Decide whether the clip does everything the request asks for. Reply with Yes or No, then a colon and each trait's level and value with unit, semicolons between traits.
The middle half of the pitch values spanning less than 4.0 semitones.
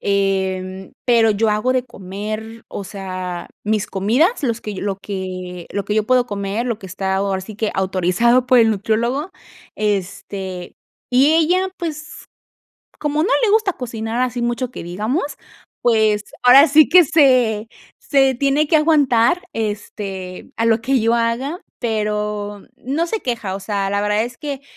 No: average, 4.5 semitones